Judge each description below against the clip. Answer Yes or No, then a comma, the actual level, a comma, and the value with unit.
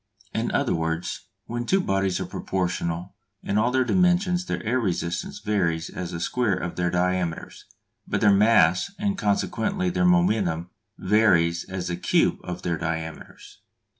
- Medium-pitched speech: No, very low, 95 Hz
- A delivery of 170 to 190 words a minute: No, average, 155 wpm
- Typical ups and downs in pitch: No, wide, 5.8 semitones